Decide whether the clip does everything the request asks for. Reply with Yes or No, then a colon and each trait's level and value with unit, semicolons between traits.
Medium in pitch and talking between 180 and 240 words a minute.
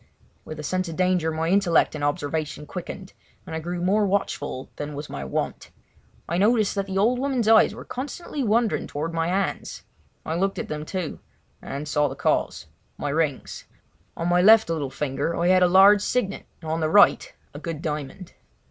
Yes: medium, 175 Hz; average, 190 wpm